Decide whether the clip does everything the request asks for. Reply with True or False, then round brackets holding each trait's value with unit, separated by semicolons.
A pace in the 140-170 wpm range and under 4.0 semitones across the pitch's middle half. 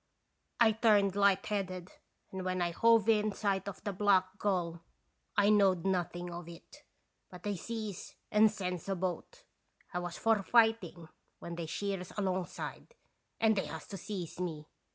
True (155 wpm; 2.8 semitones)